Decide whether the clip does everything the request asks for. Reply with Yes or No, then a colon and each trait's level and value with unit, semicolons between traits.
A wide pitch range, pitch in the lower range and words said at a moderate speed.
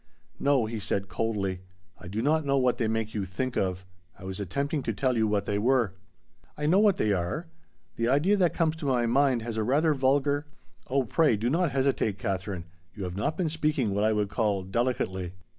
No: wide, 5.7 semitones; low, 120 Hz; fast, 215 wpm